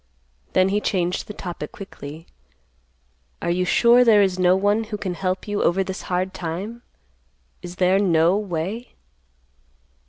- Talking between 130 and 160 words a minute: Yes, average, 150 wpm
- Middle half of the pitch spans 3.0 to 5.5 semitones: No, narrow, 2.6 semitones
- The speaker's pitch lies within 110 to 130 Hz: No, medium, 185 Hz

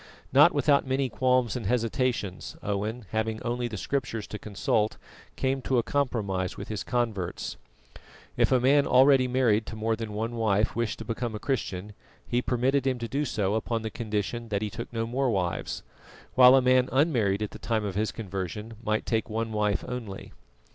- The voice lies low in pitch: Yes, low, 115 Hz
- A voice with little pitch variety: No, average, 3.0 semitones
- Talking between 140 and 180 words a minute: No, average, 190 wpm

